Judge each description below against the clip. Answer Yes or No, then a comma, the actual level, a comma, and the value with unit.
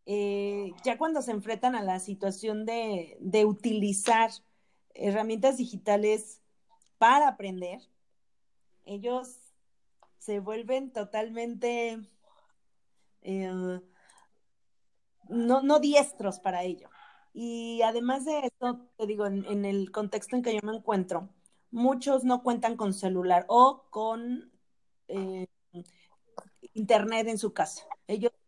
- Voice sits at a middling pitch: No, high, 220 Hz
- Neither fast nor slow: No, slow, 110 wpm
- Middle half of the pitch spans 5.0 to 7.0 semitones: No, average, 3.5 semitones